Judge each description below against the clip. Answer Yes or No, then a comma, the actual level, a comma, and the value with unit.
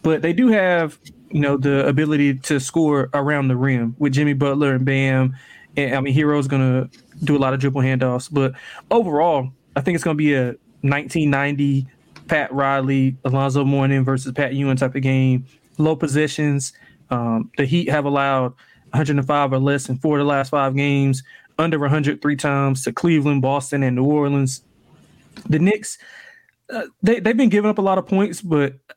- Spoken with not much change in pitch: Yes, narrow, 2.2 semitones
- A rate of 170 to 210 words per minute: Yes, average, 190 wpm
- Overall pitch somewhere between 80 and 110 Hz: No, medium, 140 Hz